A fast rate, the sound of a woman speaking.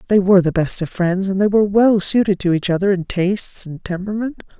Yes: fast, 235 wpm; female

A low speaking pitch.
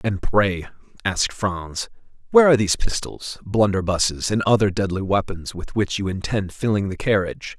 Yes: low, 100 Hz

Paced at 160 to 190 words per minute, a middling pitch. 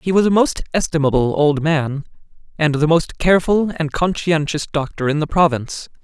Yes: average, 170 wpm; medium, 160 Hz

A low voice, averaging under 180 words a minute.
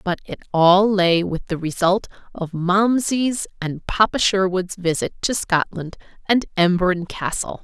No: medium, 185 Hz; average, 140 wpm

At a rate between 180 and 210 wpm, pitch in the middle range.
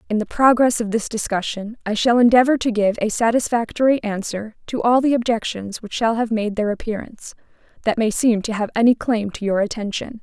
No: average, 200 wpm; high, 225 Hz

